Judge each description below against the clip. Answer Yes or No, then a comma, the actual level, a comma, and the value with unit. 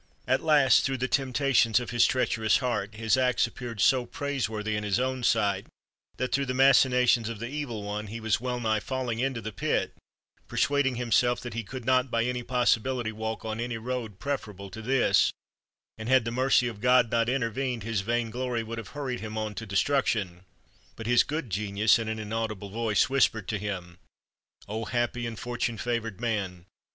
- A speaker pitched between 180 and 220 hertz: No, low, 115 Hz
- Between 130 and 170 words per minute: No, average, 190 wpm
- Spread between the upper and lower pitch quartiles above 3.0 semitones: No, average, 2.7 semitones